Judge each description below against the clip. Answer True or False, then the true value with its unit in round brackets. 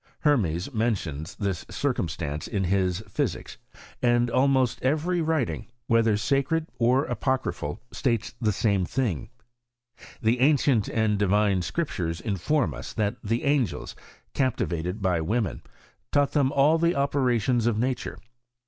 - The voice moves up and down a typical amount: False (5.7 semitones)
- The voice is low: True (115 Hz)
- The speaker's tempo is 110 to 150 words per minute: True (135 wpm)